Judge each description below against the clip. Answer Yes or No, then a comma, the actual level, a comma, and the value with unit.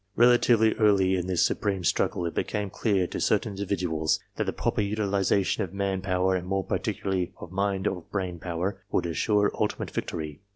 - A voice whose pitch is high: No, very low, 95 Hz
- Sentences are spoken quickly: No, average, 175 wpm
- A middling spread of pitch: No, narrow, 2.0 semitones